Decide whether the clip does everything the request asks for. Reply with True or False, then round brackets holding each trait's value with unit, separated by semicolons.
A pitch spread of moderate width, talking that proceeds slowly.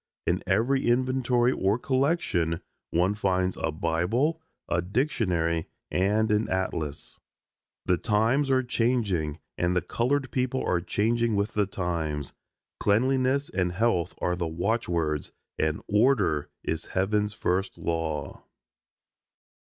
False (5.8 semitones; 120 wpm)